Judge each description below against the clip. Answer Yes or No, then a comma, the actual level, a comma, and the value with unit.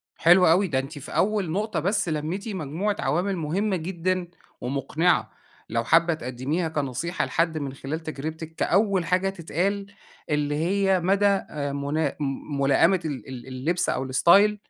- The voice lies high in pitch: No, medium, 165 Hz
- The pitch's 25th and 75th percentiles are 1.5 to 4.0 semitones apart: No, average, 4.7 semitones